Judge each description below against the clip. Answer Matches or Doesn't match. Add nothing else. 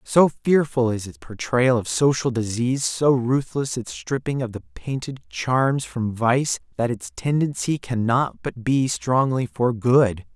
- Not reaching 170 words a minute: Matches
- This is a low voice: Matches